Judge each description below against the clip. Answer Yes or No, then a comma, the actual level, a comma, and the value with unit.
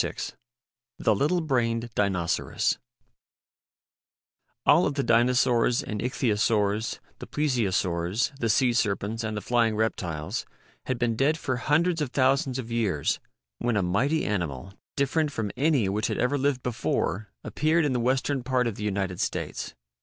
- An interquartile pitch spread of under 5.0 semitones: Yes, average, 4.4 semitones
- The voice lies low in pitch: Yes, low, 120 Hz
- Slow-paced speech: No, average, 150 wpm